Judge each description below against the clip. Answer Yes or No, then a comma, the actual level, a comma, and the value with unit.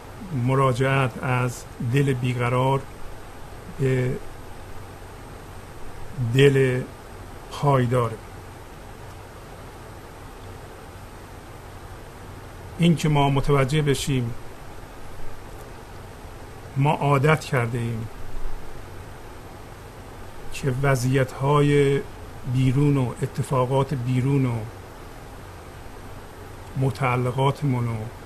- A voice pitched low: Yes, low, 115 Hz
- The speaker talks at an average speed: No, slow, 55 wpm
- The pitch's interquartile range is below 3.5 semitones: No, average, 5.1 semitones